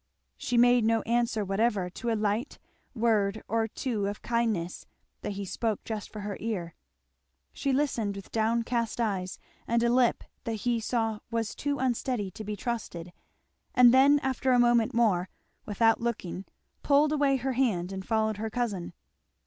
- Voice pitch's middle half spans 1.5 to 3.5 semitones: Yes, average, 2.8 semitones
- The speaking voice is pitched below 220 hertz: No, high, 225 Hz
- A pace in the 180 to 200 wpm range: No, average, 165 wpm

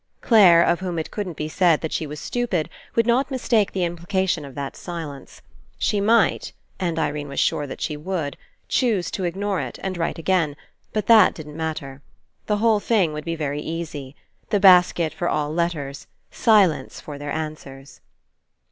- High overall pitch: No, medium, 170 Hz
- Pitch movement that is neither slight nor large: Yes, average, 4.4 semitones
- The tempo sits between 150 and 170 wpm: No, average, 185 wpm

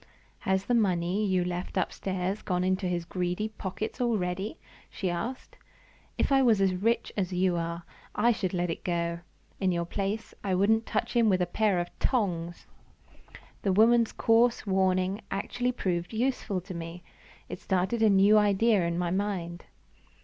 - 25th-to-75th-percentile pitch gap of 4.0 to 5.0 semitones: No, average, 3.3 semitones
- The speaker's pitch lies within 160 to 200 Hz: Yes, high, 190 Hz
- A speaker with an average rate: Yes, average, 165 wpm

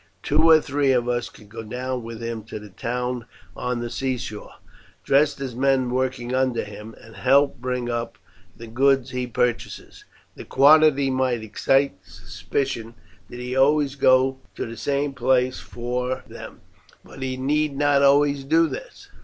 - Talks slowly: No, average, 160 wpm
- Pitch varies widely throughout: No, narrow, 2.6 semitones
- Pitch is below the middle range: Yes, low, 130 Hz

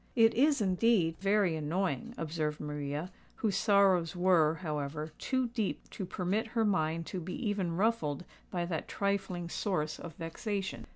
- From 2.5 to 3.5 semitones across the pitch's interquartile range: No, average, 4.3 semitones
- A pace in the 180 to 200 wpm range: No, average, 150 wpm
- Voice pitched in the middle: Yes, medium, 180 Hz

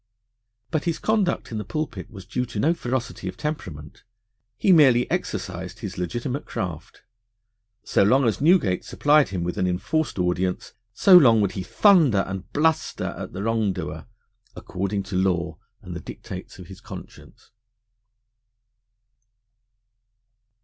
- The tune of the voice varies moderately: No, wide, 8.2 semitones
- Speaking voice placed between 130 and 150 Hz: No, low, 105 Hz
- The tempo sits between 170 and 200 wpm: No, average, 140 wpm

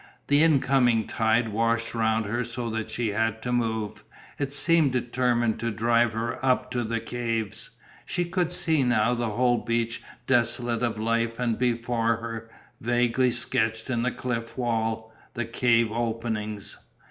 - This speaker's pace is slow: No, average, 155 wpm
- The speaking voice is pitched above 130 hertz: No, low, 115 Hz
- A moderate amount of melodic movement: No, narrow, 1.5 semitones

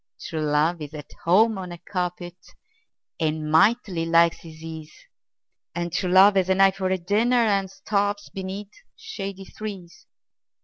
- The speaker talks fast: No, average, 150 wpm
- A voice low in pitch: No, medium, 185 Hz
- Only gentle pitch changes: No, average, 3.2 semitones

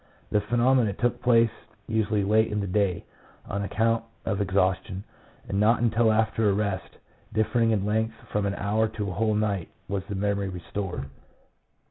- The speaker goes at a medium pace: Yes, average, 165 wpm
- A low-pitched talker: Yes, low, 105 Hz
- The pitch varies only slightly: Yes, narrow, 2.0 semitones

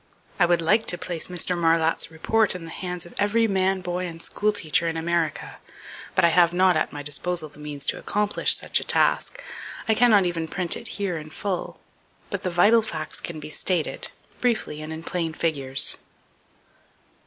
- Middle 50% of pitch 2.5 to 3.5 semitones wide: Yes, average, 3.0 semitones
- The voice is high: No, medium, 175 Hz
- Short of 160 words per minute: No, average, 190 wpm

